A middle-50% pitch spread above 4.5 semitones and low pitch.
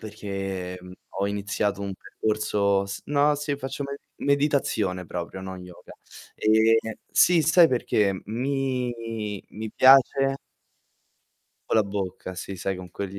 Yes: wide, 5.4 semitones; low, 105 Hz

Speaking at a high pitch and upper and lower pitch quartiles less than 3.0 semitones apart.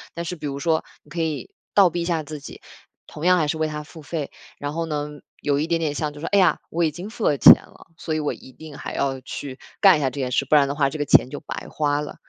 No: medium, 150 Hz; narrow, 2.5 semitones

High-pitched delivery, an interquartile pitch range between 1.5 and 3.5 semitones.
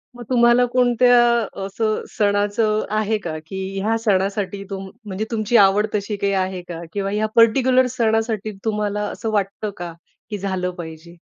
Yes: high, 210 Hz; narrow, 2.4 semitones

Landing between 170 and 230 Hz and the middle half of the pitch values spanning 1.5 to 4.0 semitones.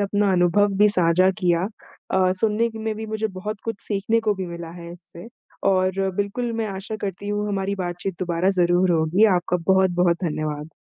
Yes: high, 190 Hz; average, 2.8 semitones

